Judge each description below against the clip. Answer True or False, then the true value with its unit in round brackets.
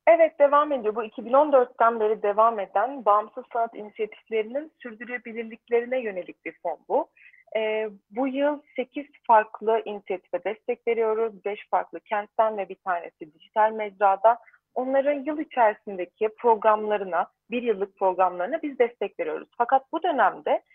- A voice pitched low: False (230 Hz)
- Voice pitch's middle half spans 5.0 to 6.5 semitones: False (4.2 semitones)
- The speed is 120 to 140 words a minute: True (130 wpm)